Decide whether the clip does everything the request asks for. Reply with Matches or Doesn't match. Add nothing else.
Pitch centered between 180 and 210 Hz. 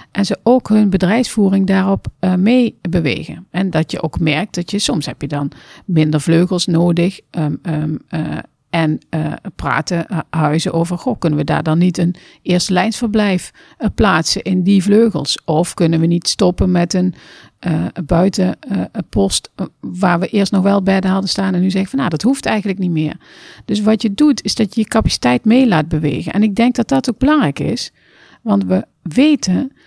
Matches